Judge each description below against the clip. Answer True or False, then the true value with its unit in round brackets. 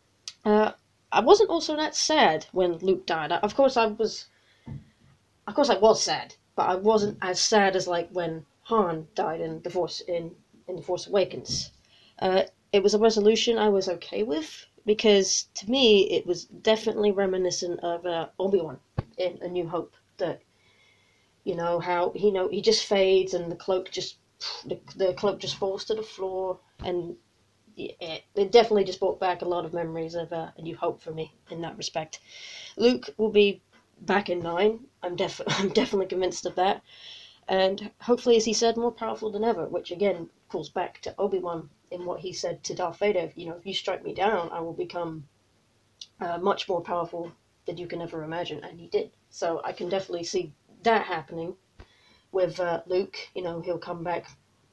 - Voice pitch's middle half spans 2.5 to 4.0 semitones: True (3.5 semitones)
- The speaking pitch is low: False (185 Hz)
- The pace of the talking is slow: False (195 wpm)